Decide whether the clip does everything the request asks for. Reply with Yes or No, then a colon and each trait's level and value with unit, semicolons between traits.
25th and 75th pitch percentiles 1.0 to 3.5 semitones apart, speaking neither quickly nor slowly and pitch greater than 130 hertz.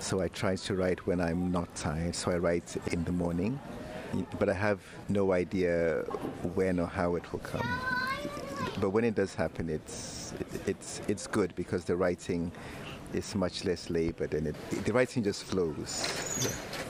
No: average, 3.2 semitones; average, 175 wpm; very low, 90 Hz